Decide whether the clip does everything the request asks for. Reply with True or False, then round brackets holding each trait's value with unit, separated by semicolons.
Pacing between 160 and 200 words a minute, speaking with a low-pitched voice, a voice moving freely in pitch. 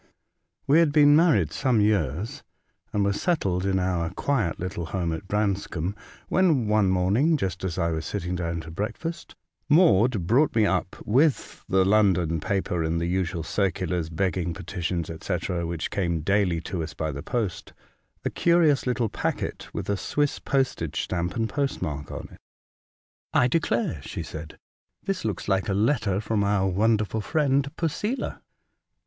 True (165 wpm; 95 Hz; 5.9 semitones)